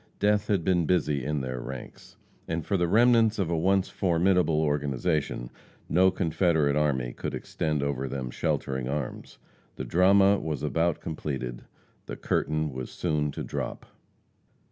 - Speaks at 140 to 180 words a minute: Yes, average, 145 wpm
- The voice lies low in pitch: Yes, very low, 80 Hz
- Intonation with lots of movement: No, average, 4.7 semitones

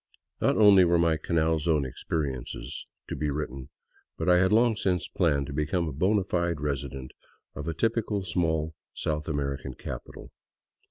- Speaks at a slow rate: No, average, 165 wpm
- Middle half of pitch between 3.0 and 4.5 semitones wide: Yes, average, 4.0 semitones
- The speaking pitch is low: Yes, very low, 80 Hz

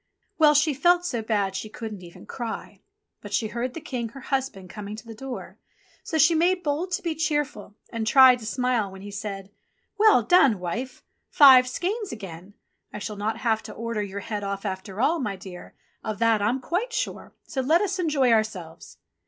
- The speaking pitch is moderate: No, high, 230 Hz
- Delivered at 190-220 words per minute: Yes, average, 195 wpm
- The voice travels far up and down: Yes, wide, 6.1 semitones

